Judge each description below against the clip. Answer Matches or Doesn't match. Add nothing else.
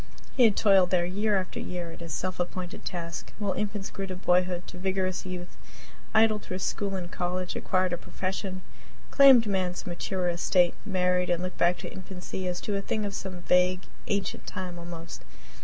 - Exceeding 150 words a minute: Matches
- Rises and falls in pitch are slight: Matches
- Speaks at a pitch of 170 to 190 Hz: Matches